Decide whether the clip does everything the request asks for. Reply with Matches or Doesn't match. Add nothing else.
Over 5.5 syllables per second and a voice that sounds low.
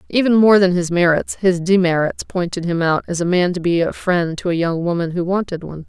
Doesn't match